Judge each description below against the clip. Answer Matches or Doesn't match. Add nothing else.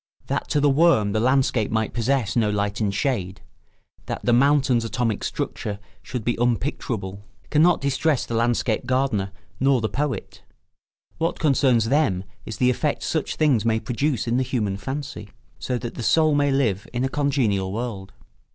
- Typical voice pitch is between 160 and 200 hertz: Doesn't match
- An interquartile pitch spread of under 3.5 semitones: Doesn't match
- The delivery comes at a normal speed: Matches